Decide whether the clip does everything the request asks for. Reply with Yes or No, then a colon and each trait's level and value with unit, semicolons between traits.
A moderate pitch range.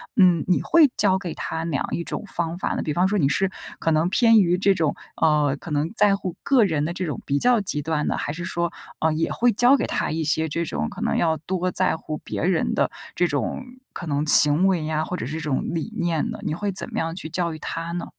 Yes: average, 3.3 semitones